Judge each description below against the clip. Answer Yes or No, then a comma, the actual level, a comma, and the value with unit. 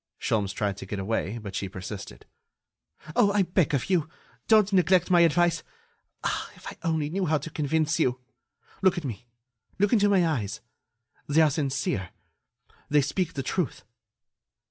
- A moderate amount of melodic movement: No, wide, 7.6 semitones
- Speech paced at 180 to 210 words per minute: No, average, 165 wpm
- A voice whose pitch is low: No, medium, 155 Hz